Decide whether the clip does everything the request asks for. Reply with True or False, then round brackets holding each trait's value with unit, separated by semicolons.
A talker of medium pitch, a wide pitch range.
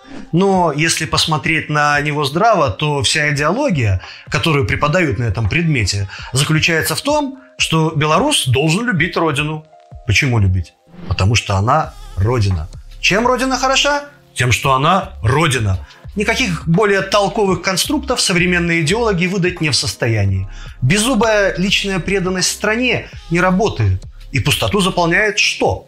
True (160 Hz; 7.9 semitones)